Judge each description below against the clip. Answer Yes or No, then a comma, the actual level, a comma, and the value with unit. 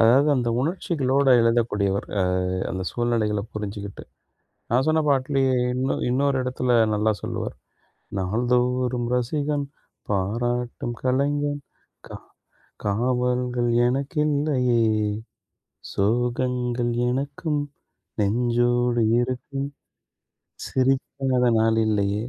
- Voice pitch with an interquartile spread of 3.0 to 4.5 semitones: No, narrow, 2.6 semitones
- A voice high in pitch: No, low, 125 Hz